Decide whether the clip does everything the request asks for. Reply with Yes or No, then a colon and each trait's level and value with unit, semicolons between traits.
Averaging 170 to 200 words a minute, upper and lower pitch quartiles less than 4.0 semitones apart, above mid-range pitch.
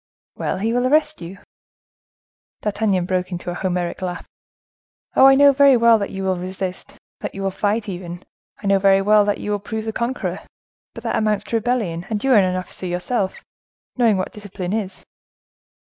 Yes: average, 190 wpm; average, 3.3 semitones; high, 200 Hz